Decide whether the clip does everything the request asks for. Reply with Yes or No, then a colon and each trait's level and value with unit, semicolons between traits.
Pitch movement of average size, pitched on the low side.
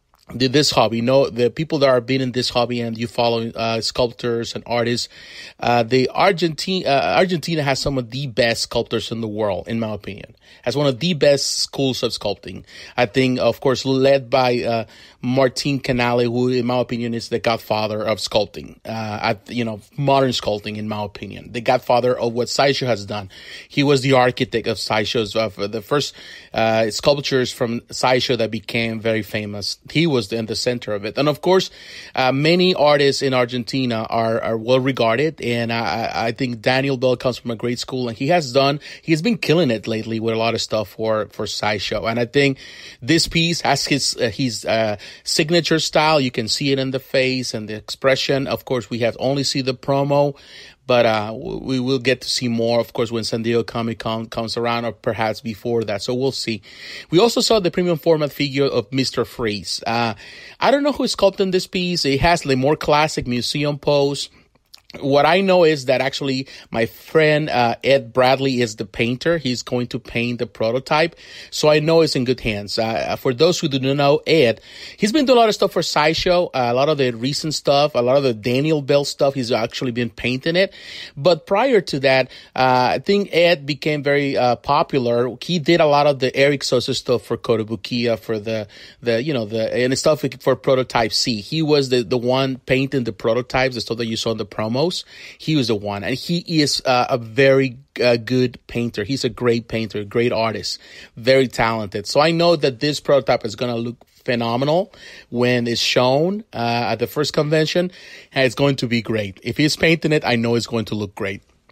Yes: average, 3.7 semitones; low, 125 Hz